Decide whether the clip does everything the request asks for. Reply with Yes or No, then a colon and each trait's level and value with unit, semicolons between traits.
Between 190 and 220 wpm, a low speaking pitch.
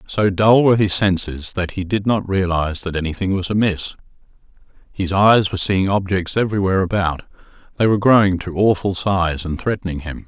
No: average, 170 wpm; very low, 95 Hz